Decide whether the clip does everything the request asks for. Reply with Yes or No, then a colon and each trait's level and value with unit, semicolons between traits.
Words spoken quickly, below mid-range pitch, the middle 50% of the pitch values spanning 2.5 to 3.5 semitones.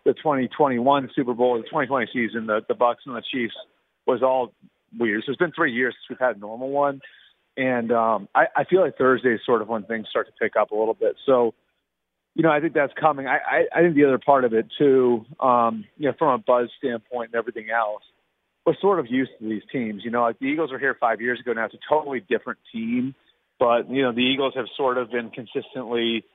Yes: fast, 245 wpm; low, 125 Hz; average, 2.9 semitones